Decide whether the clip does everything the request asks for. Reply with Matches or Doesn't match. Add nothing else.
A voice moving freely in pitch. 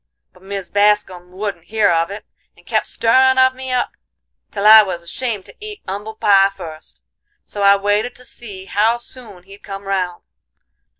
Doesn't match